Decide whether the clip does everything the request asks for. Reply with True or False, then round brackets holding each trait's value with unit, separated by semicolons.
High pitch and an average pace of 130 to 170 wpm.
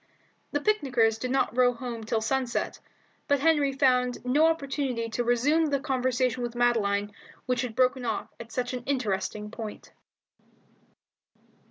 True (250 Hz; 150 wpm)